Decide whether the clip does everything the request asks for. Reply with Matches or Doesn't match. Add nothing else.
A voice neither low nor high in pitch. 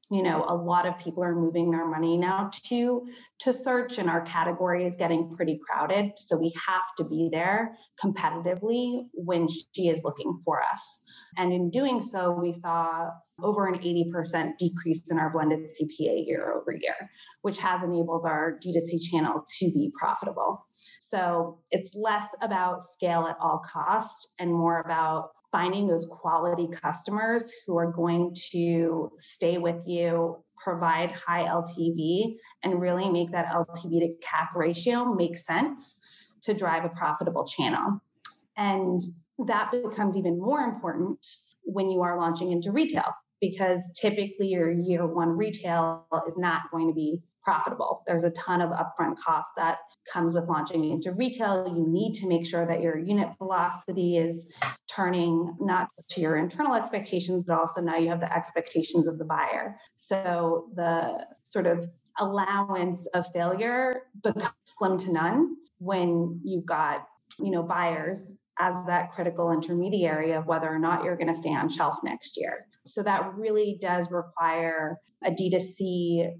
Matches